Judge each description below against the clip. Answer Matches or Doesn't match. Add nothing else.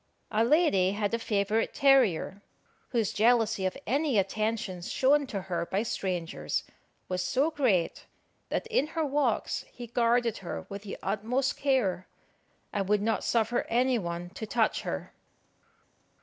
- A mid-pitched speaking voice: Doesn't match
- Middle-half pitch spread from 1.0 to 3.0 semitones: Doesn't match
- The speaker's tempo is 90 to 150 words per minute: Matches